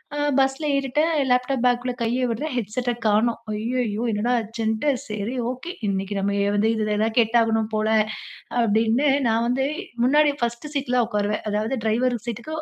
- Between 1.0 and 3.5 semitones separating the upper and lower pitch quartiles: Yes, average, 2.9 semitones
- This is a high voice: Yes, high, 235 Hz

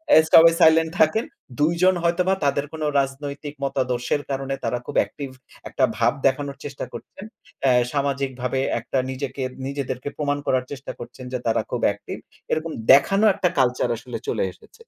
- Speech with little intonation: No, average, 3.2 semitones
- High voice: No, medium, 140 Hz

